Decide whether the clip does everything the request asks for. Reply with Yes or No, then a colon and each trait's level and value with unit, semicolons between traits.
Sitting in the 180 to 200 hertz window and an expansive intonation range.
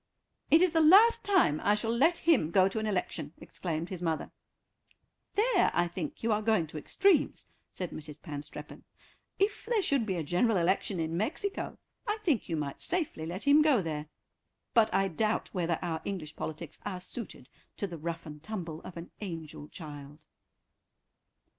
Yes: medium, 185 Hz; wide, 8.5 semitones